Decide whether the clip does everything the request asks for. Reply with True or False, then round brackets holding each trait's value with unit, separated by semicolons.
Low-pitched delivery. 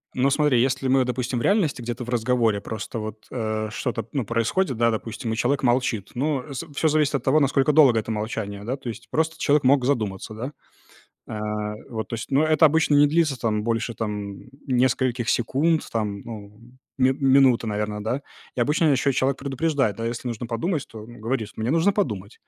True (125 Hz)